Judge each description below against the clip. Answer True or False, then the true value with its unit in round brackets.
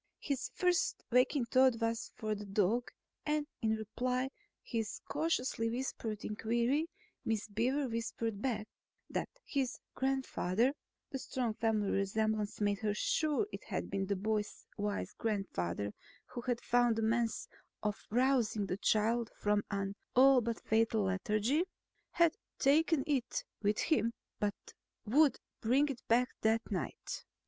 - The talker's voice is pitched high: True (230 Hz)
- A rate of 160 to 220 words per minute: False (140 wpm)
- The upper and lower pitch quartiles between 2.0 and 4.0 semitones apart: True (3.6 semitones)